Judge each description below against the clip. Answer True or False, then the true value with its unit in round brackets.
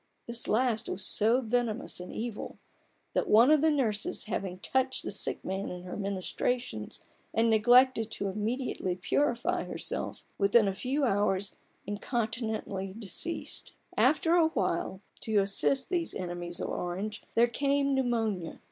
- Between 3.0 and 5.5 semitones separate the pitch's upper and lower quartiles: True (4.6 semitones)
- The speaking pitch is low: False (220 Hz)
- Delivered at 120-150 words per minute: True (140 wpm)